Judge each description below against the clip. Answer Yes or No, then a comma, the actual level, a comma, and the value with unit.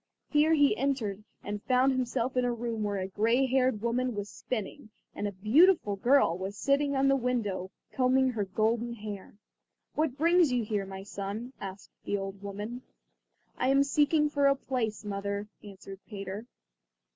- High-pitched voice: Yes, high, 235 Hz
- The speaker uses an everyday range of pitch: Yes, average, 4.7 semitones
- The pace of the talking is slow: No, average, 170 wpm